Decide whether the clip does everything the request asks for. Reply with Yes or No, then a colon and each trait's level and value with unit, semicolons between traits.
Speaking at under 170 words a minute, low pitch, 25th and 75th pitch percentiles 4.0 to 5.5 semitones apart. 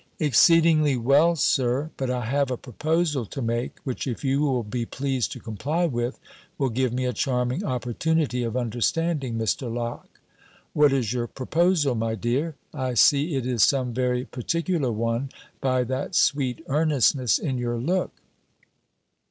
No: average, 155 wpm; low, 130 Hz; average, 3.5 semitones